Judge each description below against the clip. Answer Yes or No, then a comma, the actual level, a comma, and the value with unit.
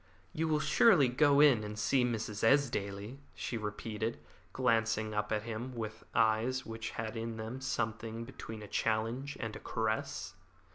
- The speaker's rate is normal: Yes, average, 155 wpm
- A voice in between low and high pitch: No, low, 115 Hz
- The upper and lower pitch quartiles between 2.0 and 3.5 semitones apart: Yes, average, 2.7 semitones